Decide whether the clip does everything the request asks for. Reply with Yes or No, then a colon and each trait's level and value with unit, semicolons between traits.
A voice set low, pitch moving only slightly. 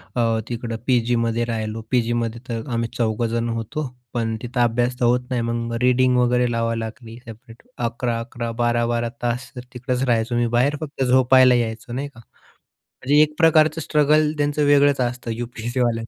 Yes: low, 120 Hz; narrow, 1.8 semitones